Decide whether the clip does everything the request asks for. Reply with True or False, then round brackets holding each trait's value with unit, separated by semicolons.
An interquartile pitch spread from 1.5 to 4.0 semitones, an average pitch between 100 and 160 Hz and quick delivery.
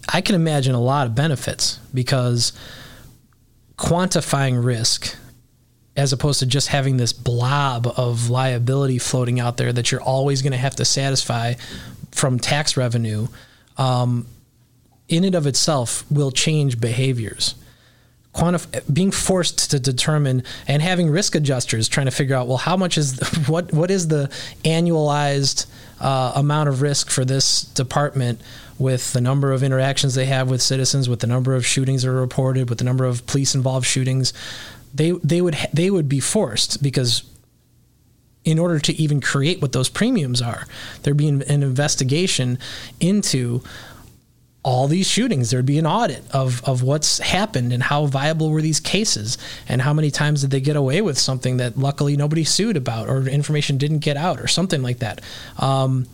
False (3.1 semitones; 135 Hz; 170 wpm)